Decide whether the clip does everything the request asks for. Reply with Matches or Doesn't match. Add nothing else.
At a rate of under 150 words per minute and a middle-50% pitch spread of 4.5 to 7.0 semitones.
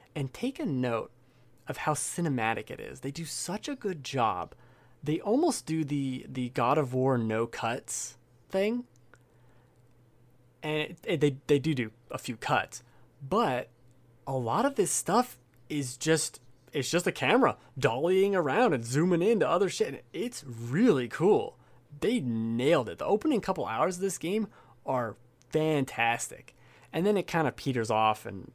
Doesn't match